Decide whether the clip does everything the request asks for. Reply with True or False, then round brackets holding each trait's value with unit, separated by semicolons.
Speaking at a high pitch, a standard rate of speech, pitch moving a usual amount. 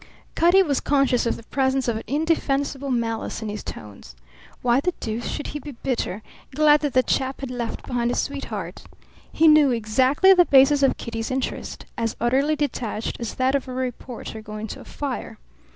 True (260 Hz; 185 wpm; 3.5 semitones)